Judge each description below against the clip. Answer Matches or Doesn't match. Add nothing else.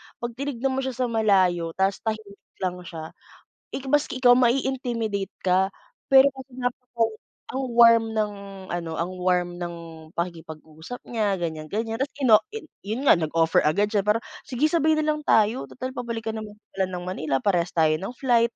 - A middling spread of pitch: Doesn't match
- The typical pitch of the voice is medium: Doesn't match